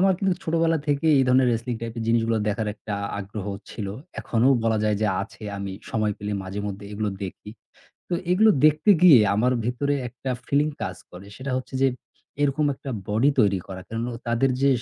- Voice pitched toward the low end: Yes, low, 115 Hz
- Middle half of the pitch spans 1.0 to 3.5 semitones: No, average, 5.2 semitones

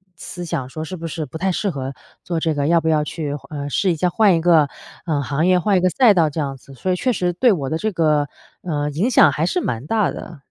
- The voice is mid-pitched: Yes, medium, 165 Hz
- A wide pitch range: No, average, 3.7 semitones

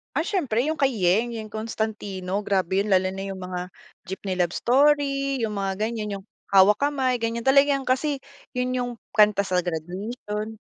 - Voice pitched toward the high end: Yes, high, 215 Hz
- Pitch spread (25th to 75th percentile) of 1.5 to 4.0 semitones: No, average, 4.9 semitones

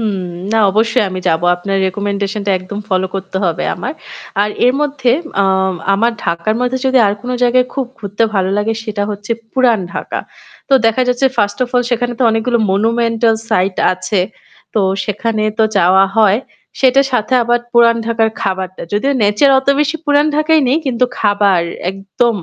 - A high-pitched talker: Yes, high, 220 Hz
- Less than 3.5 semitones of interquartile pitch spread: No, average, 3.8 semitones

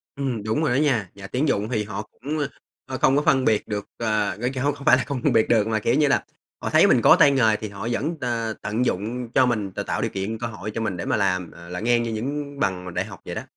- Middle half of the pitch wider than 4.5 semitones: No, average, 4.2 semitones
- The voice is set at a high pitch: No, low, 115 Hz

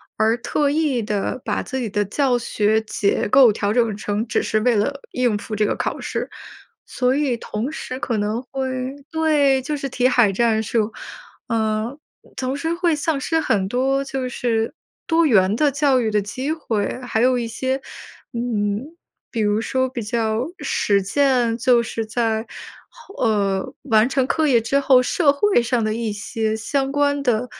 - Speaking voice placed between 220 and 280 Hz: Yes, high, 240 Hz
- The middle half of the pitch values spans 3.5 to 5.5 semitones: Yes, average, 3.8 semitones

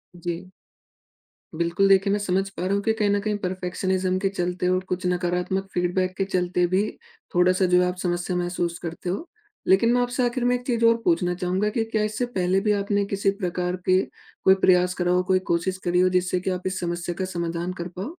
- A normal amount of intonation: No, narrow, 1.9 semitones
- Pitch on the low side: No, medium, 185 Hz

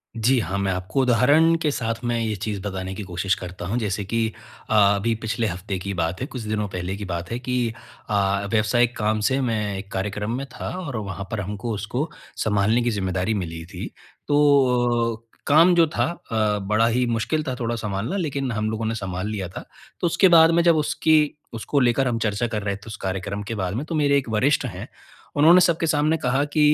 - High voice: No, low, 110 Hz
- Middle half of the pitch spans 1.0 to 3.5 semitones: No, average, 4.7 semitones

